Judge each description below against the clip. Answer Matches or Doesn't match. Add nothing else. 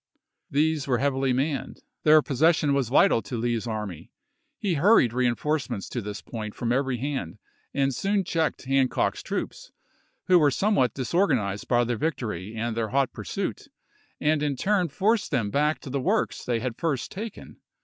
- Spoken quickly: Doesn't match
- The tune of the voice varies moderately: Matches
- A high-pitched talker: Doesn't match